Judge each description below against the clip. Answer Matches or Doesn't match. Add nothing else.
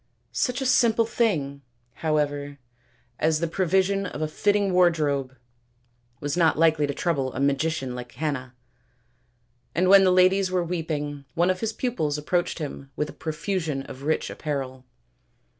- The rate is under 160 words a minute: Matches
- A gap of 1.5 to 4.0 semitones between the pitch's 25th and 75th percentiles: Doesn't match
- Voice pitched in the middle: Matches